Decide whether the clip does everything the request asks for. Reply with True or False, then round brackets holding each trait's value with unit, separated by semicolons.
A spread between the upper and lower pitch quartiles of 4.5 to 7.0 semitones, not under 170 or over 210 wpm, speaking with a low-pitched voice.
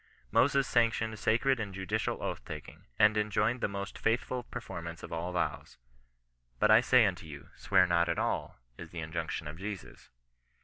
True (4.9 semitones; 175 wpm; 100 Hz)